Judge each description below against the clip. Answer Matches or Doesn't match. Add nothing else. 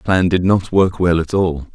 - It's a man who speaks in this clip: Matches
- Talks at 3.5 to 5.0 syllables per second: Matches